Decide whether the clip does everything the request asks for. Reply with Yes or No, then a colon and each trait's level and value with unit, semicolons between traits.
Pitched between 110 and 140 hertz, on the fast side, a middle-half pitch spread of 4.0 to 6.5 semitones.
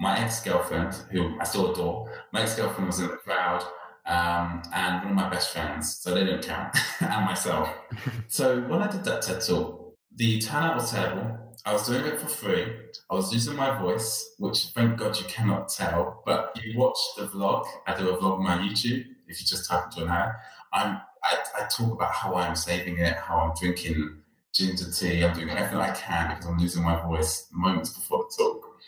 No: very low, 95 Hz; fast, 210 wpm; average, 4.7 semitones